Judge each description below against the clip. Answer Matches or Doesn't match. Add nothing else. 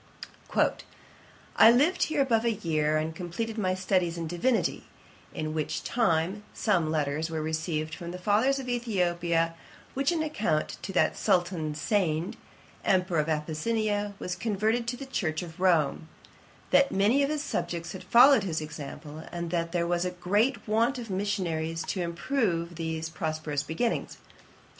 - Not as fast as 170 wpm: Matches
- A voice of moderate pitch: Matches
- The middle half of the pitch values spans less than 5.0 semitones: Doesn't match